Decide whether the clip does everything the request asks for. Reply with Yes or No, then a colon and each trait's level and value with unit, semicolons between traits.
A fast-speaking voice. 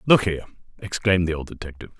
No: average, 180 wpm